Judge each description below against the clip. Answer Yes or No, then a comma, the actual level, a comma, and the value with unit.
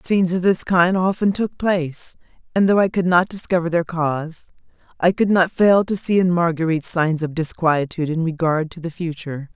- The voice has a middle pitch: Yes, medium, 170 Hz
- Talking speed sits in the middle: Yes, average, 195 wpm